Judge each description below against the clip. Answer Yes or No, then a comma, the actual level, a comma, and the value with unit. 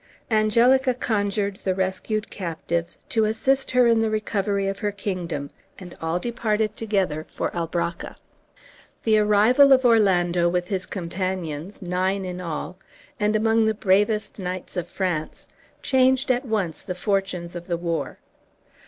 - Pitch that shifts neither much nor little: Yes, average, 3.6 semitones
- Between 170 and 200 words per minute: No, average, 145 wpm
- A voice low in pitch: No, high, 195 Hz